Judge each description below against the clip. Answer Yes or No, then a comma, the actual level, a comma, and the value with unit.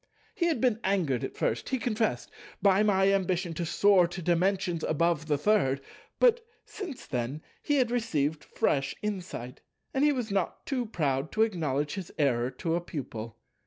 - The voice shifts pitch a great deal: Yes, wide, 6.6 semitones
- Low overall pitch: No, medium, 180 Hz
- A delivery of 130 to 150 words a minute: No, average, 165 wpm